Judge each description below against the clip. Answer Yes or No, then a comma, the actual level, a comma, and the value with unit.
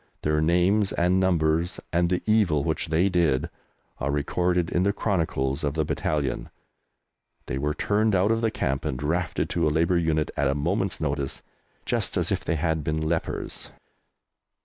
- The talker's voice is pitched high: No, very low, 80 Hz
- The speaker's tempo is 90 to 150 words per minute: No, average, 170 wpm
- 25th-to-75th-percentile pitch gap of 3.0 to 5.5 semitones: Yes, average, 3.4 semitones